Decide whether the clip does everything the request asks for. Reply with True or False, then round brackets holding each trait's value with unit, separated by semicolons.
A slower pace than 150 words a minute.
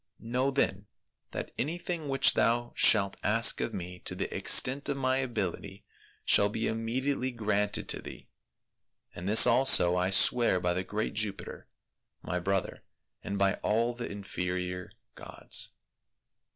True (140 wpm)